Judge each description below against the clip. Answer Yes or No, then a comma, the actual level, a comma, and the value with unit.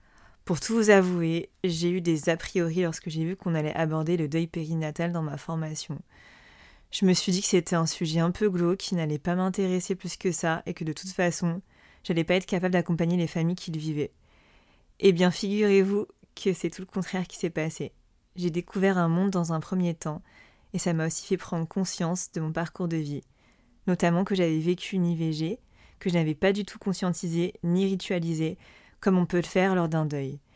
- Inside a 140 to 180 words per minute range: No, average, 215 wpm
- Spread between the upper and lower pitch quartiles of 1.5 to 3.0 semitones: Yes, narrow, 2.4 semitones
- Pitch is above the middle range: No, medium, 175 Hz